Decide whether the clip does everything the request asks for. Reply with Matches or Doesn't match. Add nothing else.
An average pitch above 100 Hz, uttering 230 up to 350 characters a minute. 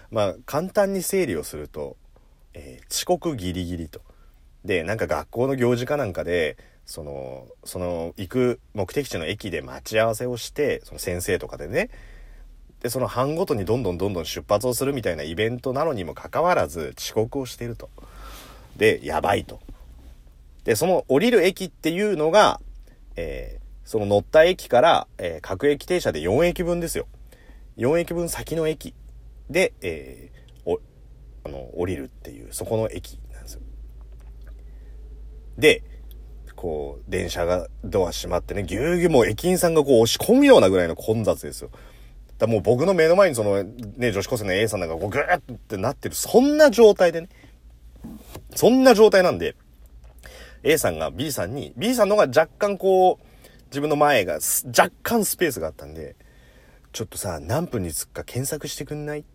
Matches